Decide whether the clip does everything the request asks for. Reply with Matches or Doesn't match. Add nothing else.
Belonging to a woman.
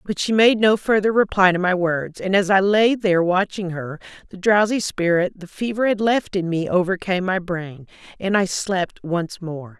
Matches